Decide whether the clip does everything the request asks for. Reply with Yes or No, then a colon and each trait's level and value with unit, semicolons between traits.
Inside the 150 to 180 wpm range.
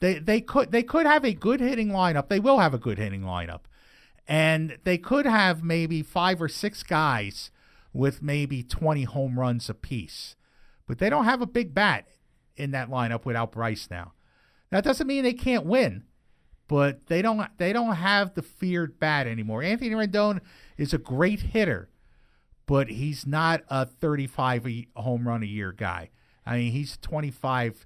Yes: average, 175 wpm